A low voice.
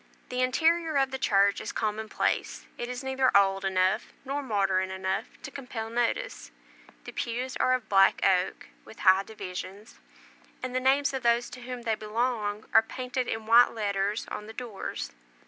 No: high, 230 Hz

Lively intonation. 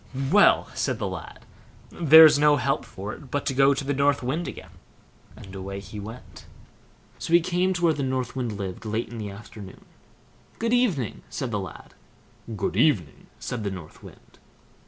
Yes: wide, 6.6 semitones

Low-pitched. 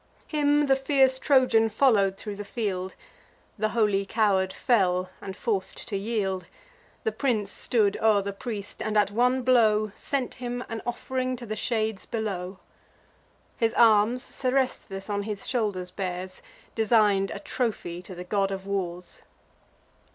No: high, 215 Hz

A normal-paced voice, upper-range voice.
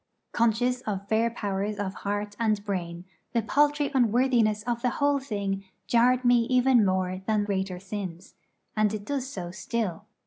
Yes: average, 160 wpm; high, 215 Hz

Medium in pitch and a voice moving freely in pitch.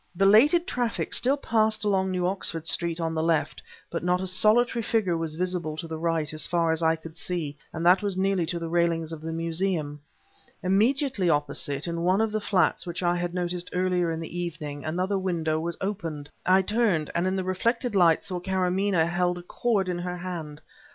No: medium, 175 Hz; average, 2.7 semitones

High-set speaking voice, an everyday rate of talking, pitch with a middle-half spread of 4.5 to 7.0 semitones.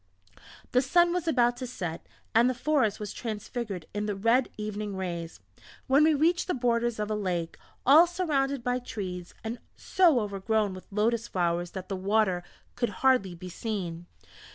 Yes: high, 220 Hz; average, 170 wpm; average, 5.1 semitones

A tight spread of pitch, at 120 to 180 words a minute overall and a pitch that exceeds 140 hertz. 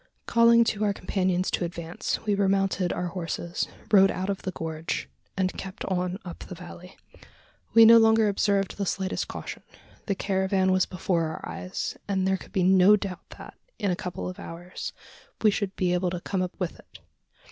No: narrow, 1.8 semitones; average, 190 wpm; high, 190 Hz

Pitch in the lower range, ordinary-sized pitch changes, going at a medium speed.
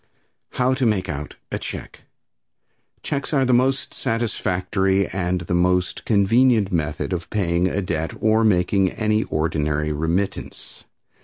No: very low, 95 Hz; average, 4.4 semitones; slow, 130 wpm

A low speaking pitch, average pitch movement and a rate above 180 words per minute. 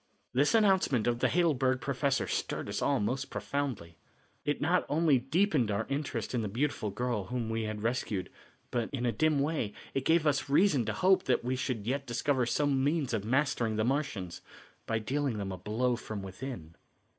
Yes: low, 130 Hz; average, 4.5 semitones; average, 190 wpm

